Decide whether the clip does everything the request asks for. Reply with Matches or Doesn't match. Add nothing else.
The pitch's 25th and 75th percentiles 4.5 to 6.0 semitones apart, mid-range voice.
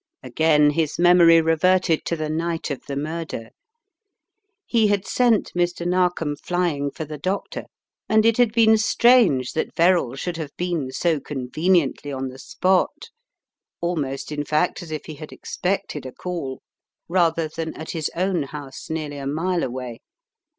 Doesn't match